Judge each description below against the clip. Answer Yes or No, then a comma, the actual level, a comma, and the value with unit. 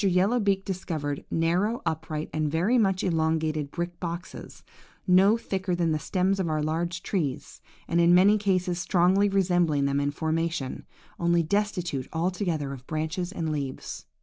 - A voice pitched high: No, medium, 170 Hz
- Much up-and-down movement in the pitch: No, average, 3.3 semitones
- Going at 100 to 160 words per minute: Yes, average, 150 wpm